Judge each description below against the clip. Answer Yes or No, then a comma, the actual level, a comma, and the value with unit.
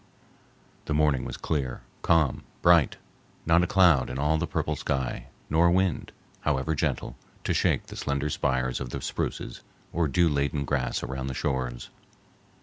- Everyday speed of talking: Yes, average, 150 wpm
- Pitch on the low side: Yes, very low, 70 Hz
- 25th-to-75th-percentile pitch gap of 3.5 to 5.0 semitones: Yes, average, 3.8 semitones